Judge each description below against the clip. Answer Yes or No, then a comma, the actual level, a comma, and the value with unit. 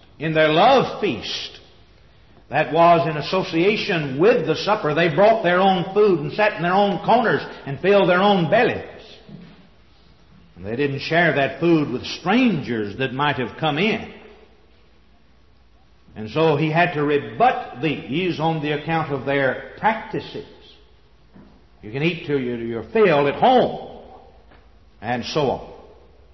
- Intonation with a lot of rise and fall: Yes, wide, 7.4 semitones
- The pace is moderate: Yes, average, 145 wpm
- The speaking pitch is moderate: Yes, medium, 150 Hz